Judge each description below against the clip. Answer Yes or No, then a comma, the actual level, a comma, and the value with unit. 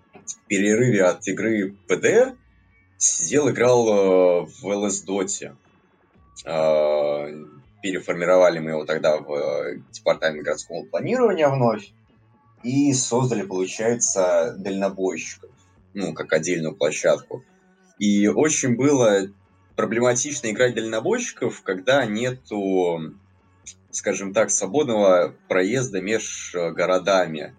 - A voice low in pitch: Yes, low, 100 Hz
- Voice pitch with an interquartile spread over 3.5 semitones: Yes, average, 4.2 semitones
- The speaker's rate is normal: No, slow, 90 wpm